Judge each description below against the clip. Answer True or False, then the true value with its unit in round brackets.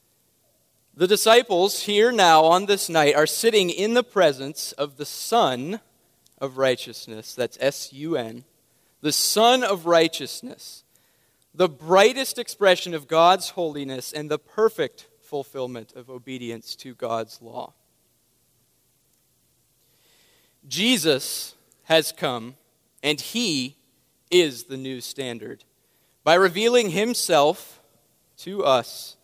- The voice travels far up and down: True (7.0 semitones)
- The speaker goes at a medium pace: False (110 wpm)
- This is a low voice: False (155 Hz)